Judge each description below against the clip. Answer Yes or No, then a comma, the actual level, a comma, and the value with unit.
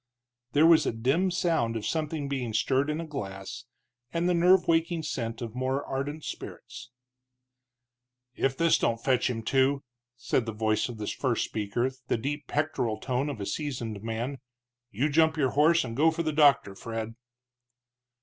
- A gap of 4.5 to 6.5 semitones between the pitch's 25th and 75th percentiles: Yes, average, 5.2 semitones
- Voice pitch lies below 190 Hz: Yes, low, 135 Hz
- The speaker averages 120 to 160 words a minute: No, average, 170 wpm